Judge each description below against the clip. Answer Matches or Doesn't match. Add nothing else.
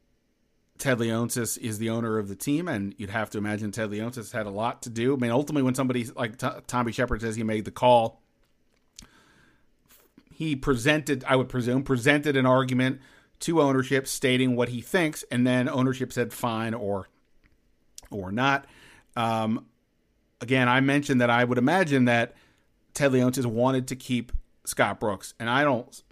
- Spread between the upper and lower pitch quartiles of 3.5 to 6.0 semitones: Doesn't match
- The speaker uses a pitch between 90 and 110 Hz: Doesn't match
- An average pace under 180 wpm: Matches